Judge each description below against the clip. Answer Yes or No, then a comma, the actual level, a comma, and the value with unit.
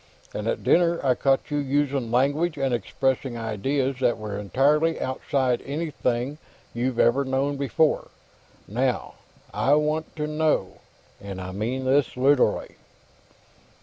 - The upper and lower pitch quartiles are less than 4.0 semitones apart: Yes, average, 3.2 semitones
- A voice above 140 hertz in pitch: No, low, 135 Hz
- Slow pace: Yes, slow, 130 wpm